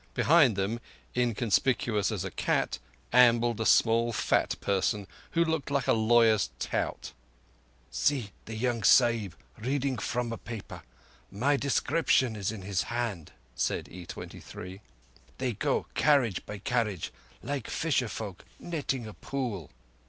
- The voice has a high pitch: No, low, 115 Hz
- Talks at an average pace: No, slow, 130 wpm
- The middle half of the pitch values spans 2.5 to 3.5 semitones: No, average, 3.9 semitones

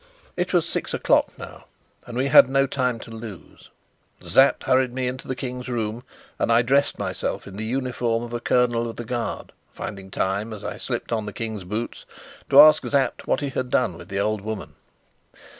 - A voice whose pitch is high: No, low, 120 Hz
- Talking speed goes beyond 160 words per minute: Yes, average, 200 wpm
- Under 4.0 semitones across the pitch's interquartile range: Yes, average, 2.8 semitones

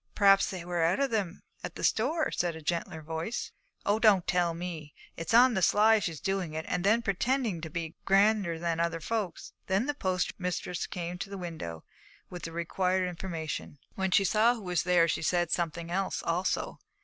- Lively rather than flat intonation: No, average, 3.1 semitones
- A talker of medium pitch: Yes, medium, 180 Hz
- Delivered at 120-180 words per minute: No, average, 195 wpm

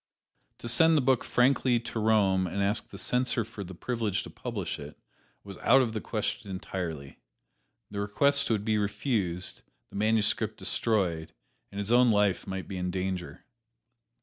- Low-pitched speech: Yes, low, 105 Hz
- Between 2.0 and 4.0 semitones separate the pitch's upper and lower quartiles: Yes, average, 3.7 semitones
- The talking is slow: No, average, 165 wpm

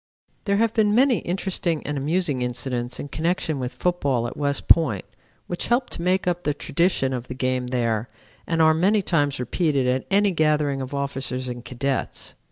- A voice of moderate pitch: Yes, medium, 145 Hz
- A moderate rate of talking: Yes, average, 180 wpm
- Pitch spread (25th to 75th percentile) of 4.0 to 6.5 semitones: Yes, wide, 5.6 semitones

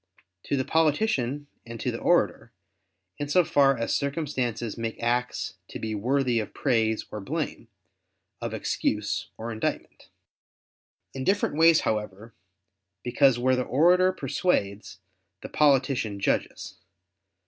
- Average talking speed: No, slow, 125 wpm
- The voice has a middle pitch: No, low, 130 Hz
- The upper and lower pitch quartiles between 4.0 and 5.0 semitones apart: Yes, average, 4.3 semitones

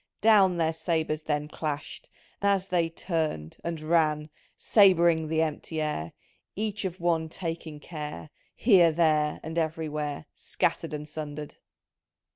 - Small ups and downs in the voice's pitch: Yes, narrow, 2.2 semitones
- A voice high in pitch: No, medium, 160 Hz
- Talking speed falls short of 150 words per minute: Yes, average, 140 wpm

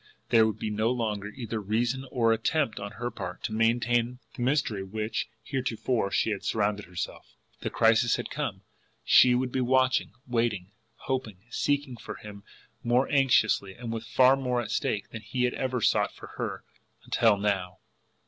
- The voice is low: Yes, low, 115 Hz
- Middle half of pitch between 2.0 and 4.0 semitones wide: Yes, average, 2.9 semitones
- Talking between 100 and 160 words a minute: No, average, 175 wpm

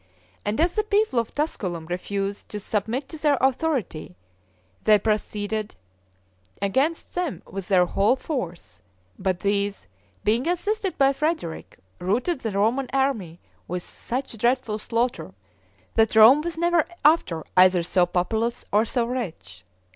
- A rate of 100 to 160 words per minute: Yes, slow, 135 wpm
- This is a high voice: Yes, high, 220 Hz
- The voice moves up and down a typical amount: No, wide, 6.2 semitones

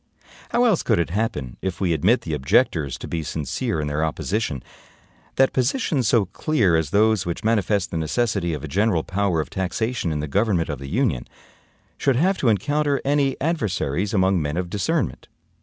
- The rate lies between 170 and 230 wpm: Yes, average, 185 wpm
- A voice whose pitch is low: Yes, very low, 95 Hz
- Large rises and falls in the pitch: Yes, wide, 6.9 semitones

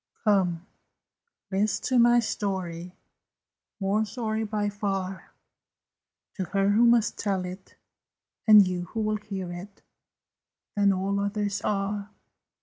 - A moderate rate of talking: No, slow, 120 wpm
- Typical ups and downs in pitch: No, narrow, 2.0 semitones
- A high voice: Yes, high, 200 Hz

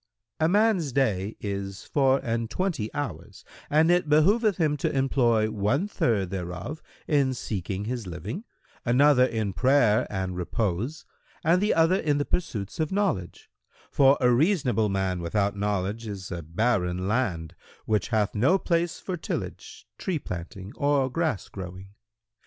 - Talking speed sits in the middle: Yes, average, 145 wpm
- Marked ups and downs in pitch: Yes, wide, 7.5 semitones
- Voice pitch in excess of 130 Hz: No, low, 120 Hz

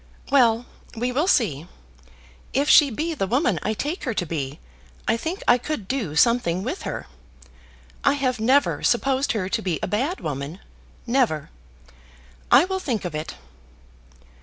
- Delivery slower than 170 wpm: Yes, average, 160 wpm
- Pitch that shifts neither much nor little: No, wide, 7.1 semitones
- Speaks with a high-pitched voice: Yes, high, 240 Hz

